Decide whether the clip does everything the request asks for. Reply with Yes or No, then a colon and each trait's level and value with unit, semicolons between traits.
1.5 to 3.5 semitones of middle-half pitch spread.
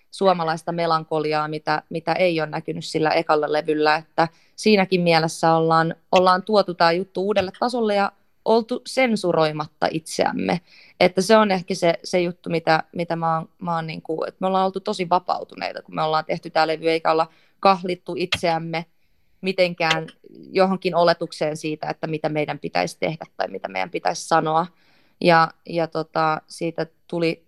Yes: narrow, 2.6 semitones